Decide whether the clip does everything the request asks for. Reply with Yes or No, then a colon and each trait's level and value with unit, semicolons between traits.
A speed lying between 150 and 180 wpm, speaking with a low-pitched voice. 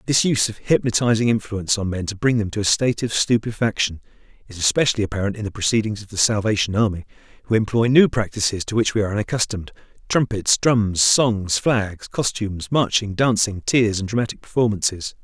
Yes: average, 175 wpm; low, 110 Hz